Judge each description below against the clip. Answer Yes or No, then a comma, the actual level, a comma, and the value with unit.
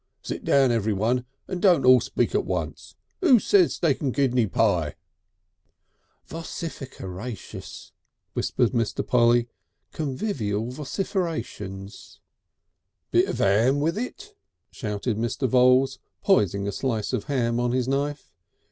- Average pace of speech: No, slow, 120 wpm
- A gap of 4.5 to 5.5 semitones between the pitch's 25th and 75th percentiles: Yes, average, 4.9 semitones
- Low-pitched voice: Yes, low, 125 Hz